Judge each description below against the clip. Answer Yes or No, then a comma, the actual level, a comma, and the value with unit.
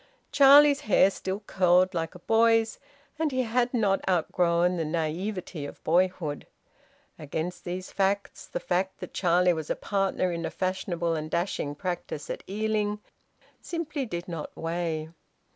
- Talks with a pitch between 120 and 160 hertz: No, medium, 185 Hz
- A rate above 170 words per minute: No, average, 145 wpm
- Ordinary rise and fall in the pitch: Yes, average, 3.8 semitones